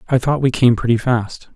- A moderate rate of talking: No, fast, 230 wpm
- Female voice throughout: No, male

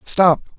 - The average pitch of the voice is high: No, medium, 175 Hz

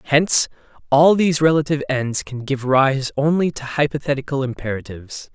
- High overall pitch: No, medium, 140 Hz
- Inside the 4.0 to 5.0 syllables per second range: No, 5.6 syllables/s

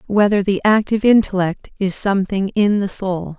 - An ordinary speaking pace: Yes, average, 160 wpm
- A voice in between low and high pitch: No, high, 200 Hz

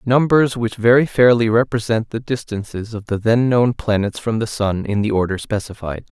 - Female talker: No, male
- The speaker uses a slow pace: No, average, 185 wpm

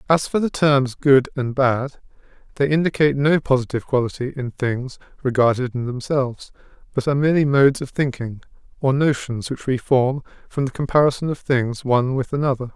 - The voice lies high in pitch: No, low, 135 Hz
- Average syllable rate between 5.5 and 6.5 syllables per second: Yes, 5.6 syllables/s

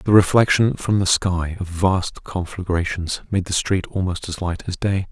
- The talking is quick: No, average, 190 wpm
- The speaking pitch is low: Yes, very low, 95 Hz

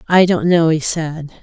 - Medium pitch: Yes, medium, 160 Hz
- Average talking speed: No, fast, 210 wpm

